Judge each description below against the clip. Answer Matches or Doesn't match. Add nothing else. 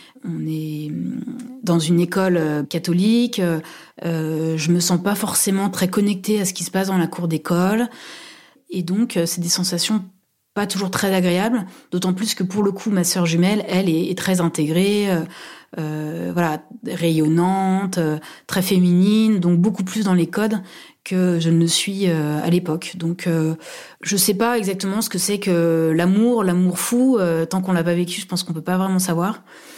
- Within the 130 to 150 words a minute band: Doesn't match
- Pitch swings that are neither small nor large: Matches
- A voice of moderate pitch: Matches